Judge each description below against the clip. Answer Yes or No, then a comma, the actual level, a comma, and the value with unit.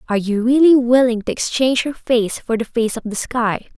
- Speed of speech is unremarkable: No, fast, 220 wpm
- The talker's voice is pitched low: No, high, 235 Hz